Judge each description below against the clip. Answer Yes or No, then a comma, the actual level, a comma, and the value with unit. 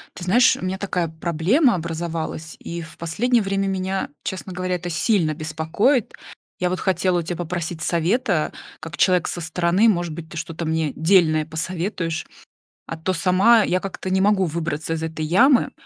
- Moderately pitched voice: Yes, medium, 175 Hz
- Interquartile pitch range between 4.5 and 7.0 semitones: No, average, 2.8 semitones